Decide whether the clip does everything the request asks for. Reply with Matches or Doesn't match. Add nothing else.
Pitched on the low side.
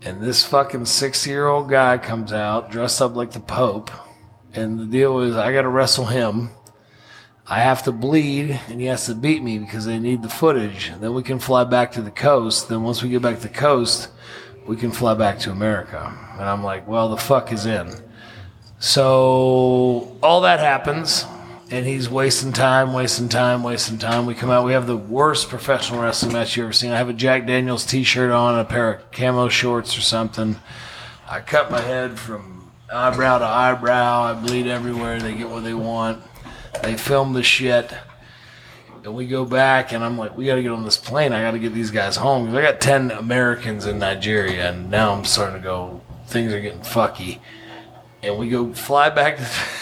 Matches